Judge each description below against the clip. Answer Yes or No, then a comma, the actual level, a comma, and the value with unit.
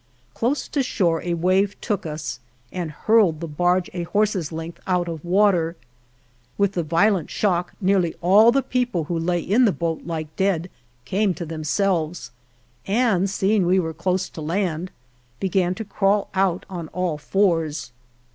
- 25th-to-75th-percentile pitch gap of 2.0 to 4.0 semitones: Yes, average, 3.1 semitones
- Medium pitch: Yes, medium, 180 Hz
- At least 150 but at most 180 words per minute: Yes, average, 160 wpm